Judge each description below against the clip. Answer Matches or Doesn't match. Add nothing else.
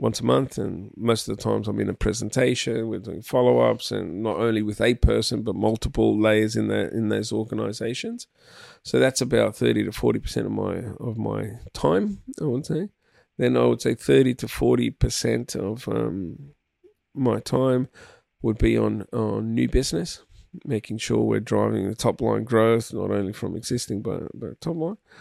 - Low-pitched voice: Matches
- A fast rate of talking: Doesn't match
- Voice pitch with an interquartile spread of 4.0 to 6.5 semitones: Doesn't match